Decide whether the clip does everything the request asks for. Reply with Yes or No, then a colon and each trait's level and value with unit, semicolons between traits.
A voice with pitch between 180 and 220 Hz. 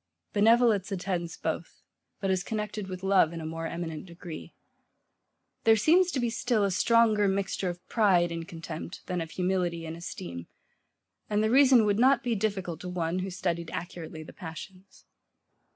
Yes: medium, 185 Hz